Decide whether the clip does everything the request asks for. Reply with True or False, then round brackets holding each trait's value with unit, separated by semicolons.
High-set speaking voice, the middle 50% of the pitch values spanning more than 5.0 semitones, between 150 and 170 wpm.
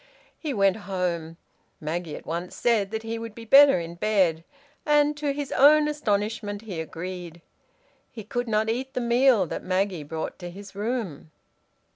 True (205 Hz; 5.6 semitones; 165 wpm)